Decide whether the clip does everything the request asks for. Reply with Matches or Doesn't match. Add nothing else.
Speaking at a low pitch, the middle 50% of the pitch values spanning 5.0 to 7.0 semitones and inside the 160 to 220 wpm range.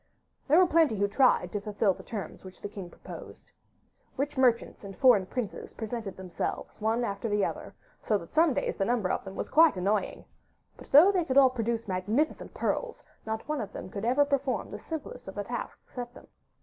Doesn't match